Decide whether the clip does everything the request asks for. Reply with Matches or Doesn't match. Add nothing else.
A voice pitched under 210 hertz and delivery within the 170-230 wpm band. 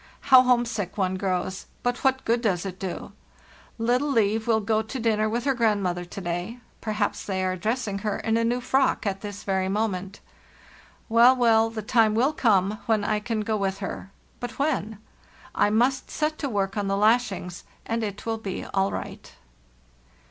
Doesn't match